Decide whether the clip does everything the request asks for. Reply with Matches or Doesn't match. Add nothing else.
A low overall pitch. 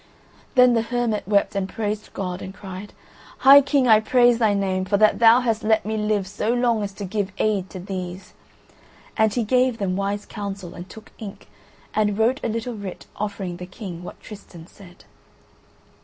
Doesn't match